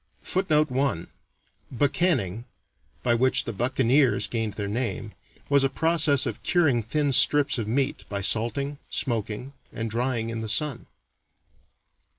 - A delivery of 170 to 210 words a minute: No, slow, 135 wpm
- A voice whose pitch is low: Yes, low, 125 Hz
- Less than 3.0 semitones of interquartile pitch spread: No, average, 4.0 semitones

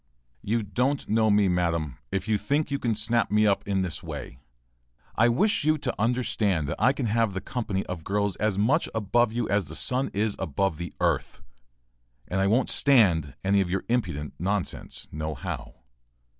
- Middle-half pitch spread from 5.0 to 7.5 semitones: No, average, 4.5 semitones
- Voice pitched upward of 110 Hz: No, low, 105 Hz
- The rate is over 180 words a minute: Yes, average, 190 wpm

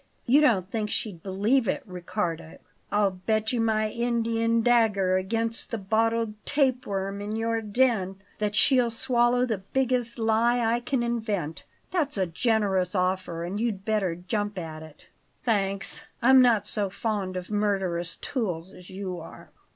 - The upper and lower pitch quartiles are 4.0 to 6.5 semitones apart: No, average, 3.6 semitones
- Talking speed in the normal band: Yes, average, 155 wpm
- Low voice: No, high, 215 Hz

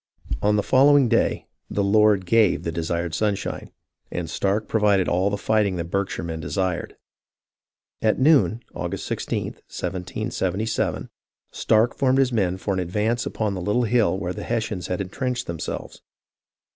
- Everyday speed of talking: Yes, average, 160 wpm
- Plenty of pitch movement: No, average, 3.8 semitones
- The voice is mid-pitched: No, low, 100 Hz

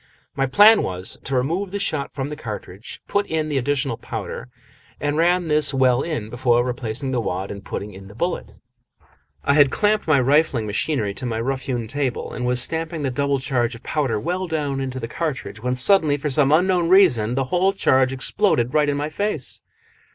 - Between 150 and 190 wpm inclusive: No, average, 200 wpm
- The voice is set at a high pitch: No, low, 135 Hz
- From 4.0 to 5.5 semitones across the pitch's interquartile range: Yes, average, 4.5 semitones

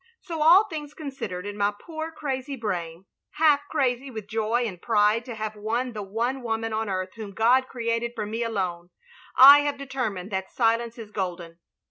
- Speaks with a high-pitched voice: Yes, high, 230 Hz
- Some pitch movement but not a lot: Yes, average, 4.3 semitones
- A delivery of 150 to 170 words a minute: No, average, 190 wpm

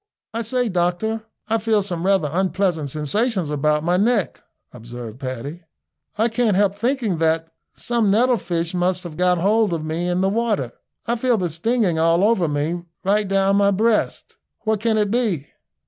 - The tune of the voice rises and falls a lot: No, average, 4.8 semitones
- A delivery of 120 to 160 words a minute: No, average, 175 wpm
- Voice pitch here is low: No, high, 190 Hz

